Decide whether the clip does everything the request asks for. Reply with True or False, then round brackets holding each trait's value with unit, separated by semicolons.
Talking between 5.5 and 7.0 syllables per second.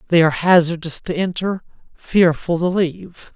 False (5.0 syllables/s)